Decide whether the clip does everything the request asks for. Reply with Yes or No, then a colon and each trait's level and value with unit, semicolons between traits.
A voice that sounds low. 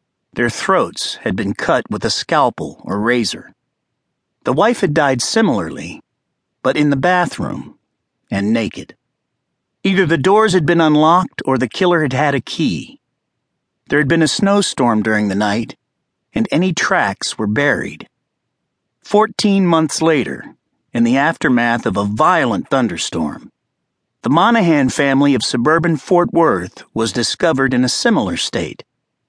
No: medium, 155 Hz